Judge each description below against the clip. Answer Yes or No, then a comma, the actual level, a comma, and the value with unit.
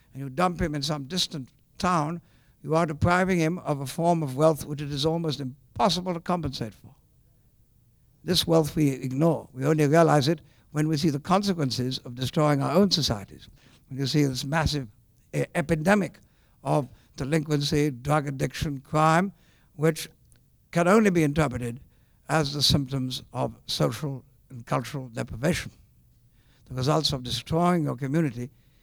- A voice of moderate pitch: Yes, medium, 145 Hz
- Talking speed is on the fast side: No, average, 155 wpm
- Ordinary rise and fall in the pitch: Yes, average, 4.0 semitones